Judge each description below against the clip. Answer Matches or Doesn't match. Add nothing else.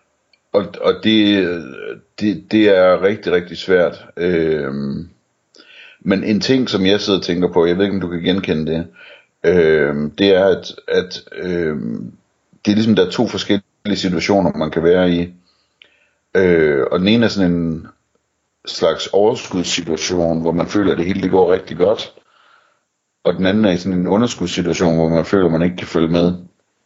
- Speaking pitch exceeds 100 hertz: Doesn't match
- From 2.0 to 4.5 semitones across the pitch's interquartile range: Matches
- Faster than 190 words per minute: Doesn't match